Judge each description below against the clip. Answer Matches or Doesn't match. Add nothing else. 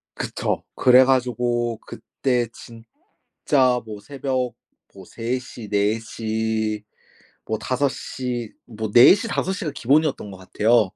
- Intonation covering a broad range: Doesn't match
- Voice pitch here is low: Matches